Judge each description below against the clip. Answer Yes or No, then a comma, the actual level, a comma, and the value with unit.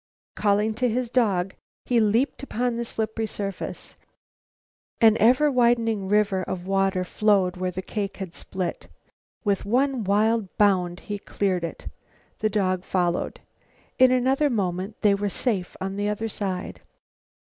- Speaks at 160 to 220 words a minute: No, average, 145 wpm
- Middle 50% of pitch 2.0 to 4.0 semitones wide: Yes, average, 3.3 semitones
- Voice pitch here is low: No, high, 205 Hz